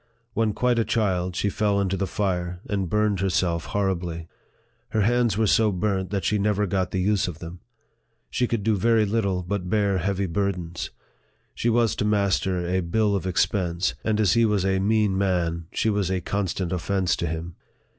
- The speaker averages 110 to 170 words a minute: No, average, 190 wpm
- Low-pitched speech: Yes, low, 100 Hz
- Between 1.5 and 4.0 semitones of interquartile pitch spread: Yes, average, 2.7 semitones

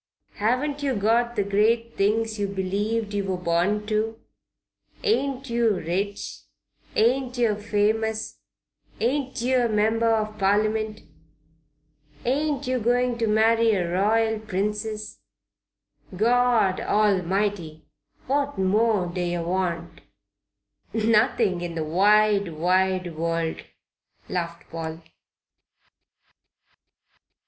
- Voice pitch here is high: Yes, high, 210 Hz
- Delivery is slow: Yes, slow, 105 wpm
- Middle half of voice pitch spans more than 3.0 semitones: Yes, average, 3.5 semitones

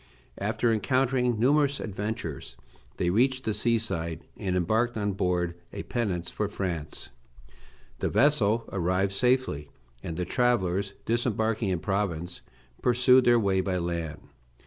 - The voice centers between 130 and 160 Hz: No, low, 105 Hz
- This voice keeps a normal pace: No, slow, 130 wpm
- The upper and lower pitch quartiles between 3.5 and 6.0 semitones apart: Yes, average, 5.2 semitones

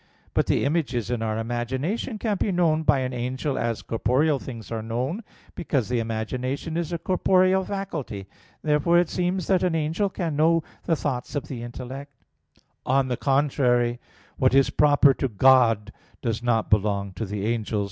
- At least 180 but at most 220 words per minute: No, average, 170 wpm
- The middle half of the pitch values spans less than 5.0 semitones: No, wide, 5.5 semitones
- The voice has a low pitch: Yes, low, 130 Hz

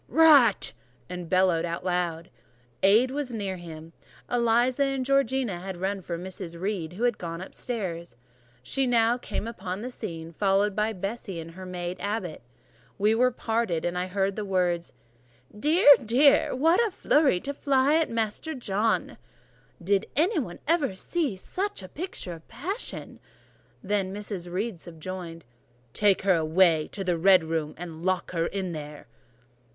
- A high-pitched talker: Yes, high, 195 Hz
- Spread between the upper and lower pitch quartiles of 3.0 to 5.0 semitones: No, wide, 5.6 semitones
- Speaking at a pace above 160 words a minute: No, average, 155 wpm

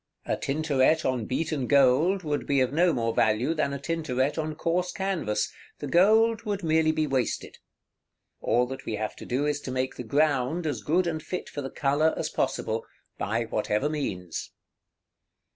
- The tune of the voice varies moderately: Yes, average, 4.1 semitones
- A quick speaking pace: No, average, 175 wpm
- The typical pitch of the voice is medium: Yes, medium, 145 Hz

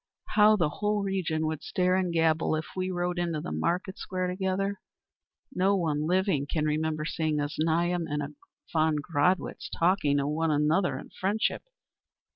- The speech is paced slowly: No, average, 165 wpm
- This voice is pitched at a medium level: Yes, medium, 170 Hz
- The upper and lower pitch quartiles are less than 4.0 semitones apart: Yes, average, 3.4 semitones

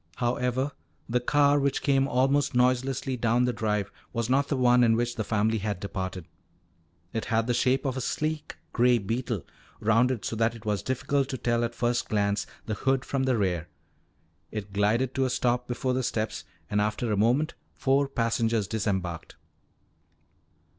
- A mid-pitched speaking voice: No, low, 120 Hz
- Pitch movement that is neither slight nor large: Yes, average, 3.2 semitones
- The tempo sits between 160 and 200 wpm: Yes, average, 175 wpm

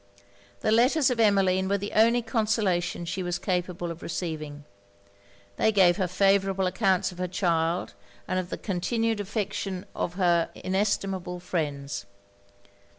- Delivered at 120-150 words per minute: Yes, average, 140 wpm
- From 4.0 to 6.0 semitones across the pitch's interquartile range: No, narrow, 2.5 semitones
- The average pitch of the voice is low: No, medium, 185 Hz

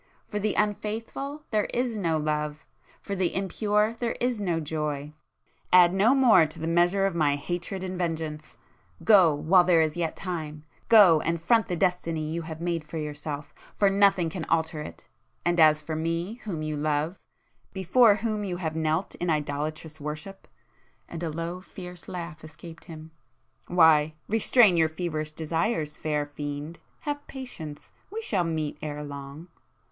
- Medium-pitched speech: Yes, medium, 165 Hz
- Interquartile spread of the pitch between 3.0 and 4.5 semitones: Yes, average, 4.0 semitones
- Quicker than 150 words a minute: No, average, 145 wpm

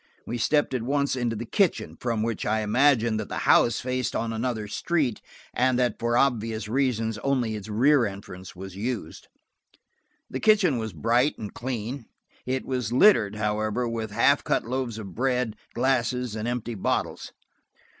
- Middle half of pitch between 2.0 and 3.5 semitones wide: Yes, average, 2.9 semitones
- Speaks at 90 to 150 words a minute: No, average, 165 wpm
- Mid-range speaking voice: No, low, 120 Hz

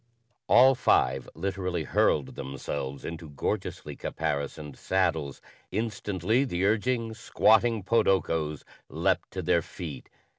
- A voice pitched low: Yes, very low, 90 Hz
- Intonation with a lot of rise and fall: Yes, wide, 6.5 semitones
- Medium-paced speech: No, slow, 105 wpm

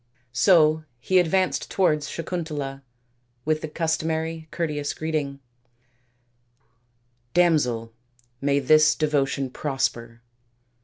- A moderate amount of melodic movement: Yes, average, 4.0 semitones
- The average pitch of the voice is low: No, medium, 150 Hz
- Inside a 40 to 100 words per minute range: Yes, slow, 90 wpm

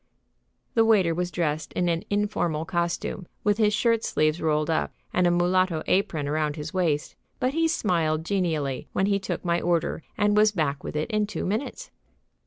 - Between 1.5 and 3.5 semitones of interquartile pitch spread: No, average, 4.7 semitones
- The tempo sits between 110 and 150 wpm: No, average, 185 wpm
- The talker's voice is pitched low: No, medium, 175 Hz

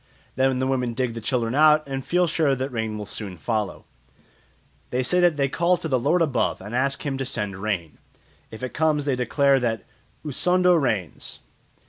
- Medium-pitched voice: No, low, 130 Hz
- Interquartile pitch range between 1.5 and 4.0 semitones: No, average, 4.6 semitones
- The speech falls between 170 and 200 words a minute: Yes, average, 190 wpm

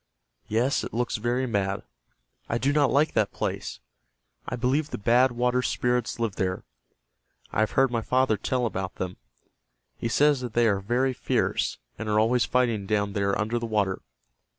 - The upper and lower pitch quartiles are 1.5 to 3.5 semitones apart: Yes, average, 3.2 semitones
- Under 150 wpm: No, average, 175 wpm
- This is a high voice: No, low, 115 Hz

